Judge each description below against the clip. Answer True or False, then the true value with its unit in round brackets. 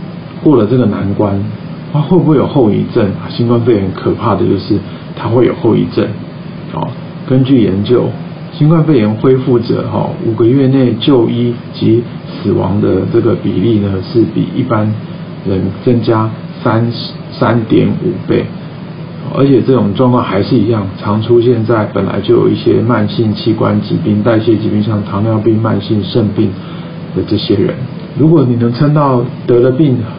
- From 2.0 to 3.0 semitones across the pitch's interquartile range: False (5.2 semitones)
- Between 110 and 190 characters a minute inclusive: False (240 characters per minute)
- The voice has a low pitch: True (120 Hz)